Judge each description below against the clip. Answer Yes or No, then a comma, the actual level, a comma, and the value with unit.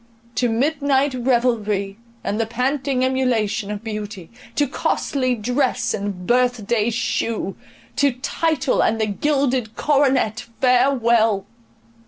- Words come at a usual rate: No, slow, 115 wpm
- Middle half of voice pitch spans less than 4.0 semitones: Yes, average, 3.6 semitones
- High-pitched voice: Yes, high, 245 Hz